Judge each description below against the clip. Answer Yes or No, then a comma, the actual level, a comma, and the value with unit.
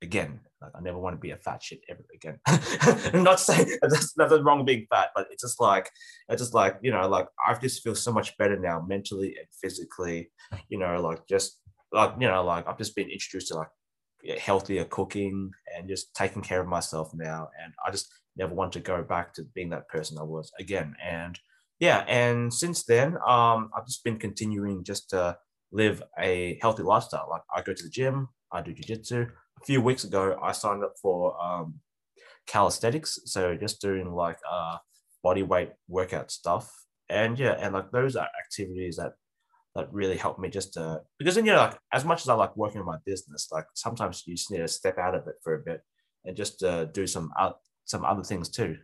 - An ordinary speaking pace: No, fast, 215 wpm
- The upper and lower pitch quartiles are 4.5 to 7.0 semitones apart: Yes, average, 5.1 semitones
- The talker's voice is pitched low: Yes, low, 100 Hz